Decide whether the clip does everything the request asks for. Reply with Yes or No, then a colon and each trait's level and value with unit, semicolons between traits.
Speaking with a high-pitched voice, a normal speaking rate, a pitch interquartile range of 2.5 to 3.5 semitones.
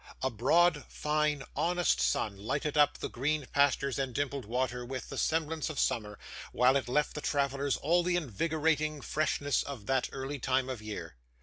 No: medium, 140 Hz; average, 175 wpm; average, 3.0 semitones